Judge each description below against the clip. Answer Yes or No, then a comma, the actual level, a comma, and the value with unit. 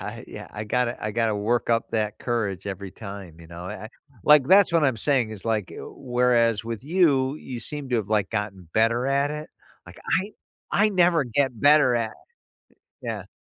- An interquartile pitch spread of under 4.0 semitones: No, average, 4.7 semitones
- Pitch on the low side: Yes, low, 115 Hz